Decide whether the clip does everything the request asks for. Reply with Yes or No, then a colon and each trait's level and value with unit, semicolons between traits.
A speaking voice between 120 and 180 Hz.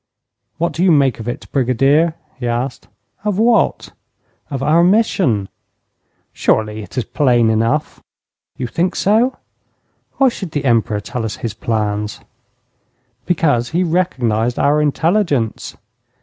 Yes: low, 135 Hz